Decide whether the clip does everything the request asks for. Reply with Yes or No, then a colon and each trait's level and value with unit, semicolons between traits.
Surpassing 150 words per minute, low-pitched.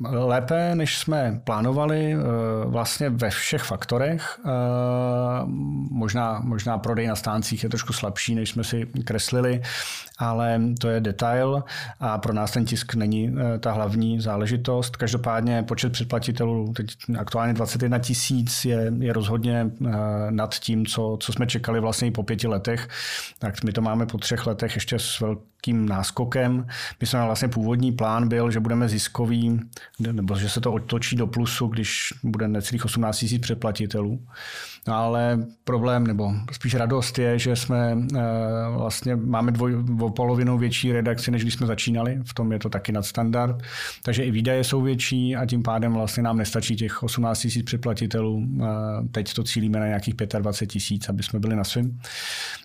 Yes: average, 160 wpm; low, 115 Hz